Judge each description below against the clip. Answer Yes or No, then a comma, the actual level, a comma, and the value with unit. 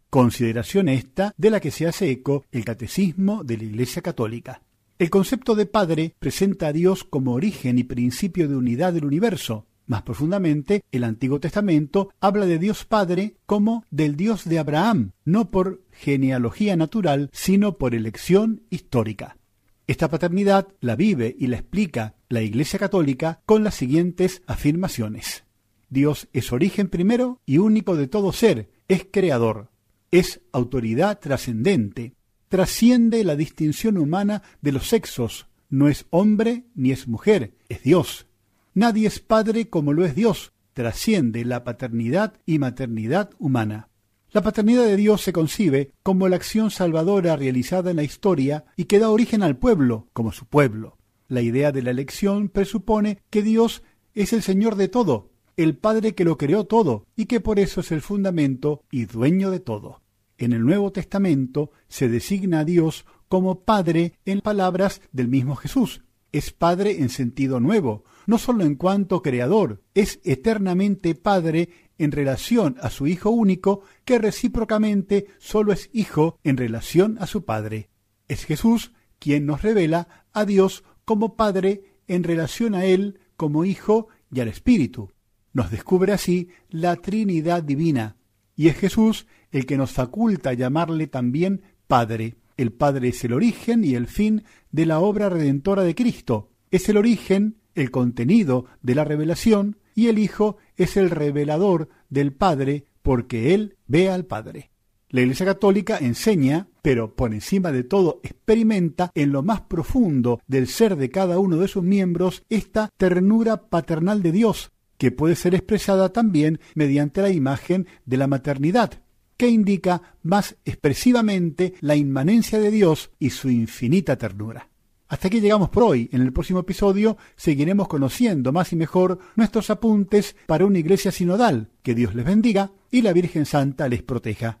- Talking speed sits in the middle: Yes, average, 155 wpm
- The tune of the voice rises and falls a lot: Yes, wide, 7.4 semitones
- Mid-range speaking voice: Yes, medium, 170 Hz